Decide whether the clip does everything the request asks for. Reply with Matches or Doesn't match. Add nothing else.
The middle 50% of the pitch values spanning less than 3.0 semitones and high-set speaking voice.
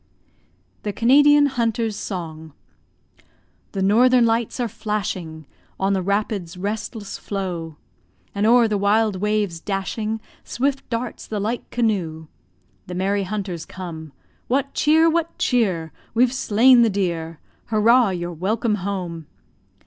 Doesn't match